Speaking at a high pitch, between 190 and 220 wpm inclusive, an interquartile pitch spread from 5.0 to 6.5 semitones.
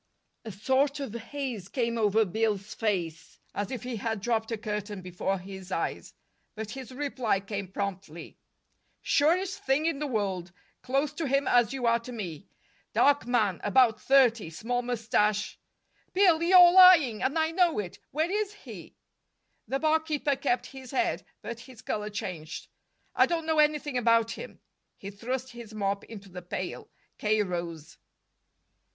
No: high, 230 Hz; average, 160 wpm; wide, 5.5 semitones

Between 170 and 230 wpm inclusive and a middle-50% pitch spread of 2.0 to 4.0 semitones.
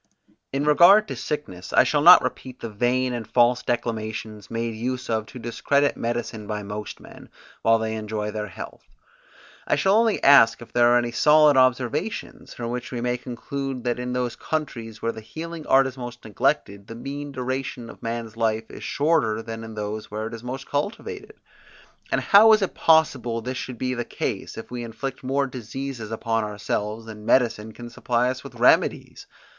Yes: average, 190 wpm; average, 3.3 semitones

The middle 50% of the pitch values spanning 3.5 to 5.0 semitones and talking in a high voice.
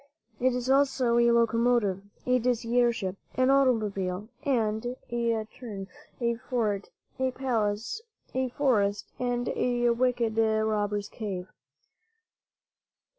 No: average, 2.8 semitones; high, 235 Hz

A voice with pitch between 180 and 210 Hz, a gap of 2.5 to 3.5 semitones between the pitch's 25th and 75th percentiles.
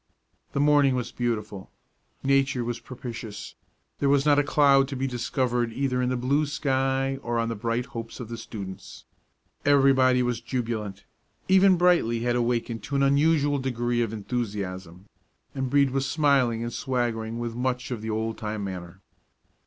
No: low, 125 Hz; average, 3.1 semitones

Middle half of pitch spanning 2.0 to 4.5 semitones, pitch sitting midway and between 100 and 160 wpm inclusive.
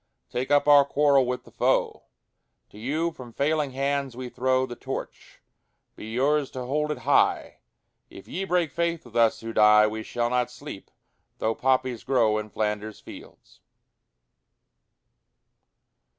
No: average, 4.1 semitones; low, 130 Hz; average, 150 wpm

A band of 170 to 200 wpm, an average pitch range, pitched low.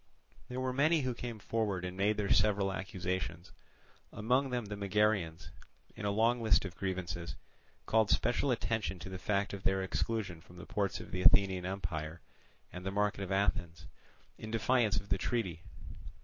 Yes: average, 175 wpm; average, 3.2 semitones; low, 100 Hz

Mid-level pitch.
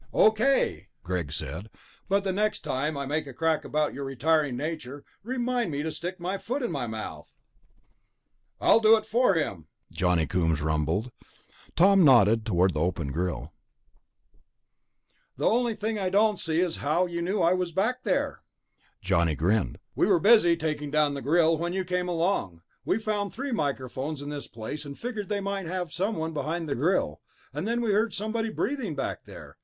Yes: medium, 160 Hz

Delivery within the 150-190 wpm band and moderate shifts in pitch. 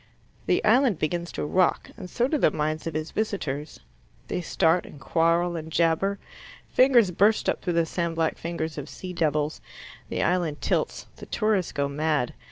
Yes: average, 175 wpm; average, 3.2 semitones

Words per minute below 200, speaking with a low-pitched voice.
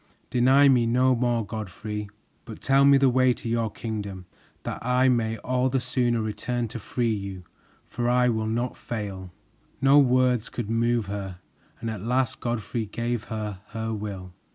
Yes: average, 170 wpm; low, 115 Hz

